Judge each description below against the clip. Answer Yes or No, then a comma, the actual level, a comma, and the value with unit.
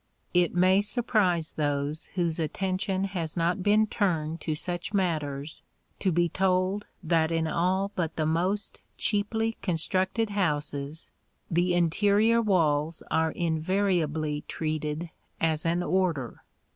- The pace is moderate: No, slow, 120 wpm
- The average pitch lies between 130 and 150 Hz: No, medium, 175 Hz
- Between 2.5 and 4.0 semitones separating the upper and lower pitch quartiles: Yes, average, 3.4 semitones